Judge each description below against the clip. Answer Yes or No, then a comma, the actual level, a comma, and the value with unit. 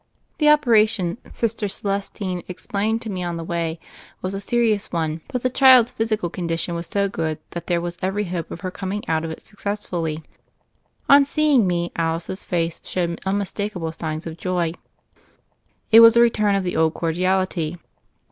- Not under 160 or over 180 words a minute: Yes, average, 175 wpm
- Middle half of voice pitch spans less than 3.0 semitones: No, average, 4.0 semitones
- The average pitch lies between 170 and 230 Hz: Yes, medium, 185 Hz